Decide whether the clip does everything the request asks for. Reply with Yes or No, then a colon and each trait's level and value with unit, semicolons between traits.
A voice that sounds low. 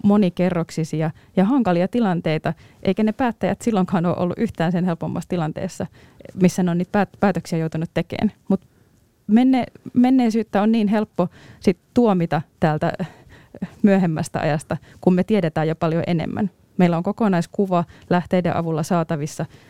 No: medium, 180 Hz